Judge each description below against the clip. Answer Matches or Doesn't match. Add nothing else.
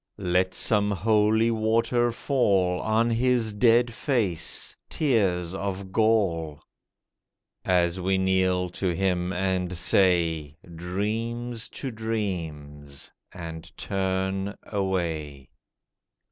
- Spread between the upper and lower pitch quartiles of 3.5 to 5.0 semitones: Matches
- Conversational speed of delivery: Doesn't match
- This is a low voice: Matches